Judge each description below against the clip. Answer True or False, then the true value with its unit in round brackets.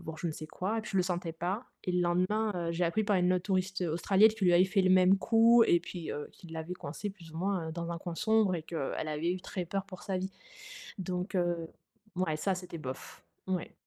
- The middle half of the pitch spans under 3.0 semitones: True (2.4 semitones)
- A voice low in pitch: False (180 Hz)